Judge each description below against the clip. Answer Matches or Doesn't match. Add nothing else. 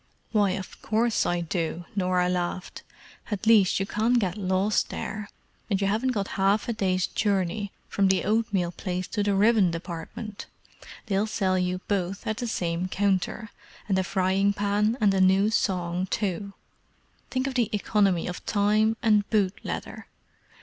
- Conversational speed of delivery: Matches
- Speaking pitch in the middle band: Doesn't match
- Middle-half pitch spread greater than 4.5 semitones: Doesn't match